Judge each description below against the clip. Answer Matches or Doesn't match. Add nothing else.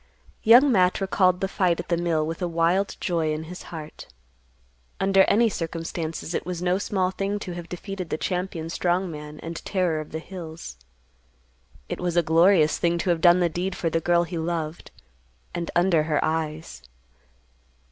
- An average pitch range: Doesn't match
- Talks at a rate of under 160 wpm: Doesn't match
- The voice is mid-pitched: Matches